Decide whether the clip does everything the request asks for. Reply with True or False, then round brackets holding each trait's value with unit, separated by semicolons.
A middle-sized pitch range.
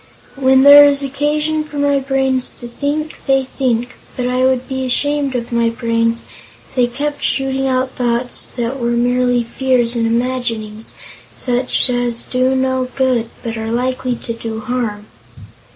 False (2.1 semitones)